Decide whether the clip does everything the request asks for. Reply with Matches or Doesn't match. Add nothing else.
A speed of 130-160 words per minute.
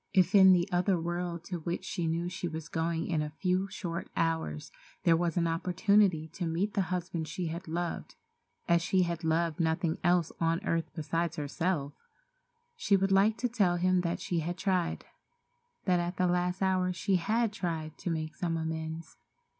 Doesn't match